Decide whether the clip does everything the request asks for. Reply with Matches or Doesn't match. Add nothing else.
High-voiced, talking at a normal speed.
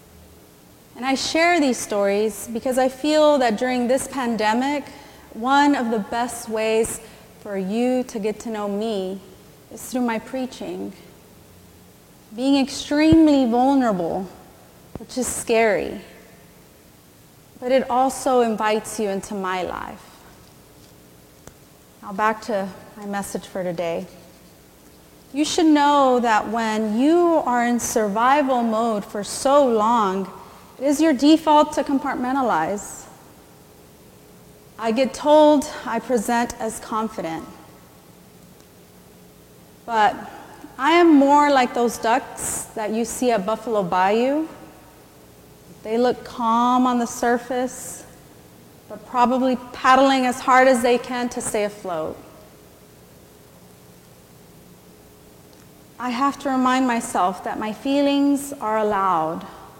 Doesn't match